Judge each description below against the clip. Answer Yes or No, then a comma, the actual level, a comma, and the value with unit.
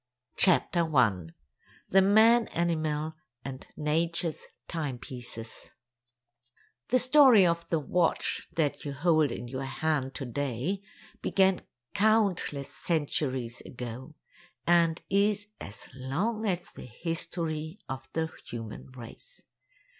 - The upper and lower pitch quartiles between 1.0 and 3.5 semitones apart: No, wide, 5.4 semitones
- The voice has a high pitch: No, medium, 160 Hz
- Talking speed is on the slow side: Yes, slow, 110 wpm